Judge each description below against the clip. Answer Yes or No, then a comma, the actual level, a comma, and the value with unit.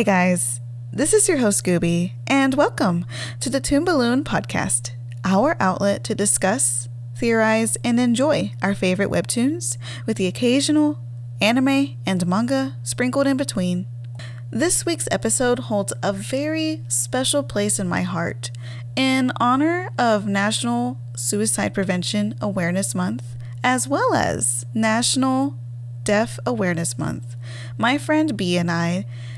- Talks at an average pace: No, slow, 130 wpm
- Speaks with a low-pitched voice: No, medium, 145 Hz